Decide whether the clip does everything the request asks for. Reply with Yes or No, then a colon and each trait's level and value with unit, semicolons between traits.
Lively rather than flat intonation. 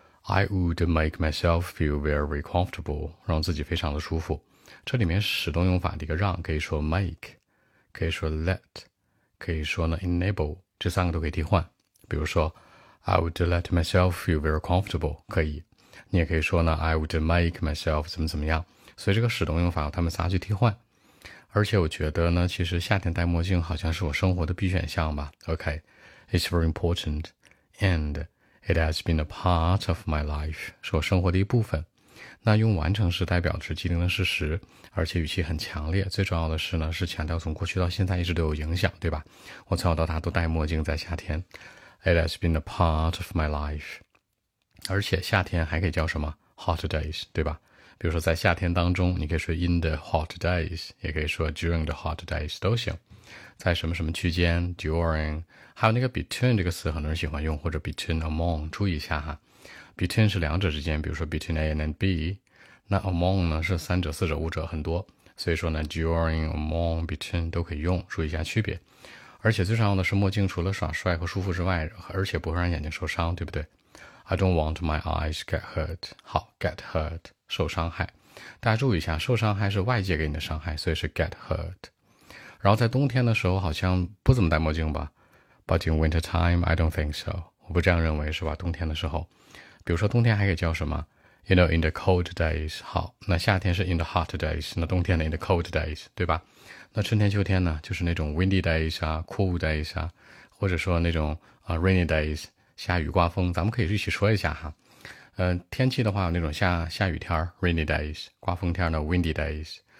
No: average, 2.9 semitones